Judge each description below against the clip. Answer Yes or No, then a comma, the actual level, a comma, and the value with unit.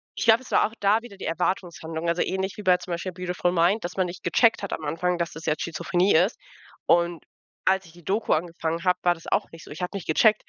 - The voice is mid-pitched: Yes, medium, 180 Hz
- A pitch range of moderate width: No, narrow, 2.3 semitones